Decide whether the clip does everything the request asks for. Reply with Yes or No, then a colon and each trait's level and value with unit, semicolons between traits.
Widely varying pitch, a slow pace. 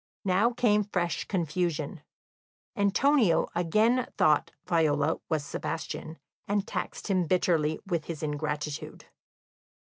No: average, 4.7 semitones; slow, 100 wpm